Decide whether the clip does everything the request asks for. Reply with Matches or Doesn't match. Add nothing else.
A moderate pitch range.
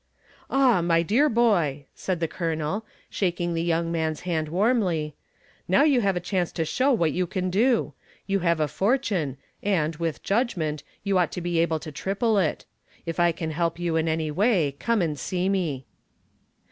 Matches